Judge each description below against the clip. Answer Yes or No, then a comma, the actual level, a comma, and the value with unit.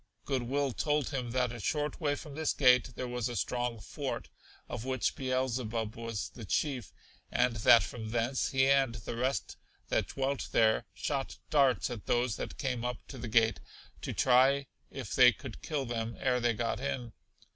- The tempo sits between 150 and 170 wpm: No, average, 185 wpm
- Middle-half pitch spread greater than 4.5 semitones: No, narrow, 2.5 semitones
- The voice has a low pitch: Yes, low, 125 Hz